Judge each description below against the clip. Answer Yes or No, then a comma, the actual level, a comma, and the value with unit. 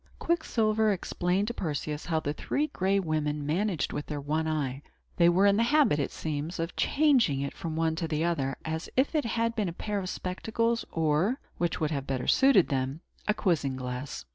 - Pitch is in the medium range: Yes, medium, 170 Hz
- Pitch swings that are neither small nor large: No, wide, 6.1 semitones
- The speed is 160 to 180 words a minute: No, average, 195 wpm